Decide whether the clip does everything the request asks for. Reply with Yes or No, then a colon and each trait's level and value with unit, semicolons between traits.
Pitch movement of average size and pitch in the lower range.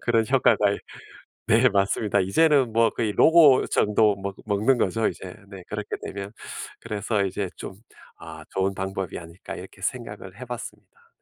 Yes: average, 3.6 semitones; low, 105 Hz